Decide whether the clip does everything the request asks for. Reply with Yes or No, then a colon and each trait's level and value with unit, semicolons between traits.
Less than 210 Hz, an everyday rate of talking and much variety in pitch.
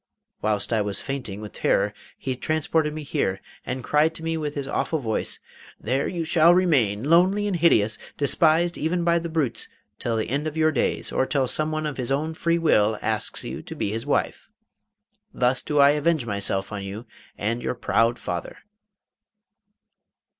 Yes: medium, 140 Hz; average, 180 wpm; wide, 6.3 semitones